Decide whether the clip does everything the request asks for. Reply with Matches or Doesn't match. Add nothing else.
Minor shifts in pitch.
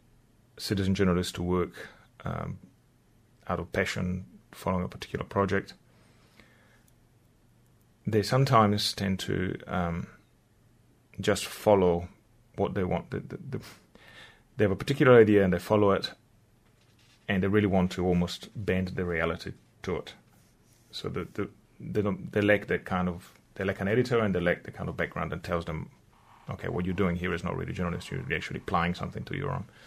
Doesn't match